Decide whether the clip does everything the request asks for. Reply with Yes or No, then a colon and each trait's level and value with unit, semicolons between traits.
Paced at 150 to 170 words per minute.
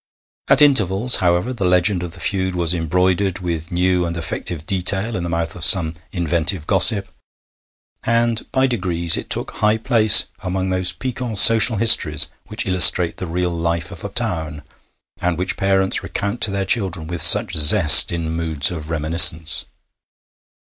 Yes: average, 160 wpm